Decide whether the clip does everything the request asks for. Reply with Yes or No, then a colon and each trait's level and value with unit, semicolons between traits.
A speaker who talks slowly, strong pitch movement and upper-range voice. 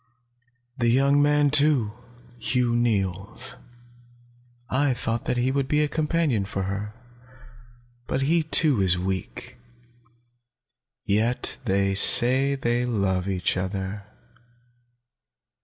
No: slow, 105 wpm; wide, 6.0 semitones; low, 120 Hz